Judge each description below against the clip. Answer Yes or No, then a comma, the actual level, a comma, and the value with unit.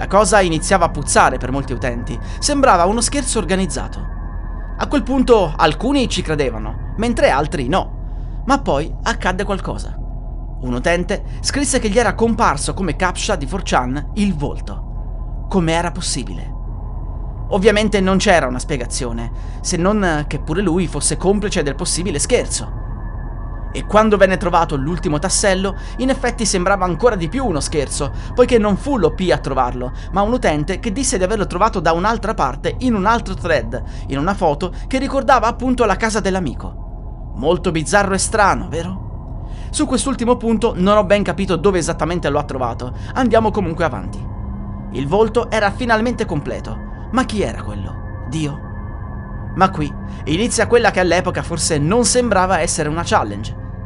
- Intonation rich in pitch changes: Yes, wide, 8.0 semitones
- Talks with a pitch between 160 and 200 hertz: Yes, medium, 185 Hz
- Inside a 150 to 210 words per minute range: Yes, average, 160 wpm